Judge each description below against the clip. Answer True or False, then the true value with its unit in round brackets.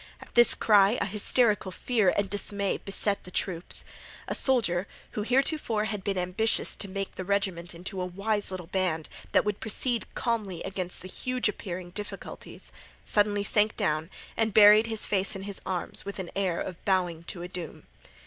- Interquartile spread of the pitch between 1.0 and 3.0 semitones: True (2.7 semitones)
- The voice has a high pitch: True (200 Hz)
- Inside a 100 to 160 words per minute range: False (175 wpm)